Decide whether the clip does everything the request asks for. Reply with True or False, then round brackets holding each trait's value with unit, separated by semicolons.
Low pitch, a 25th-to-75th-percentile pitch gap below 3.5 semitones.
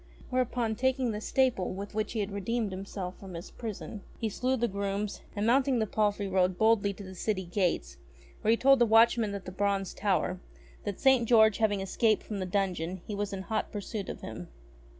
False (205 Hz; 2.9 semitones)